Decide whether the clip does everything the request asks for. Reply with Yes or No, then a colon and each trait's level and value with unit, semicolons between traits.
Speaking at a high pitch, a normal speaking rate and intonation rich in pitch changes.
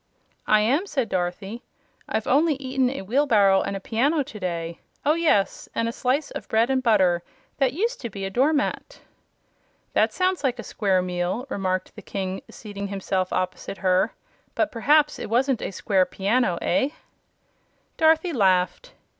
Yes: high, 225 Hz; average, 165 wpm; wide, 6.3 semitones